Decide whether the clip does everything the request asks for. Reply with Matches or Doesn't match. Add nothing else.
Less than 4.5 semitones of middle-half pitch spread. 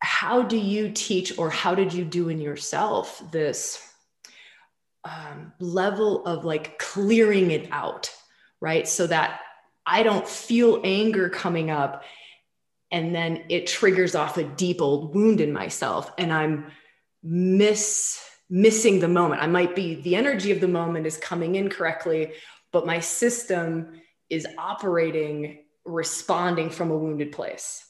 Matches